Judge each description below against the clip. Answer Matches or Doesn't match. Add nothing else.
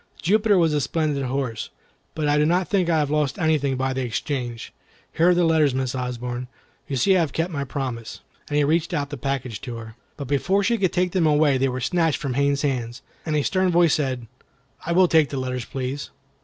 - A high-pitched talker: Doesn't match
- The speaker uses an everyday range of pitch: Matches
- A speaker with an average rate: Doesn't match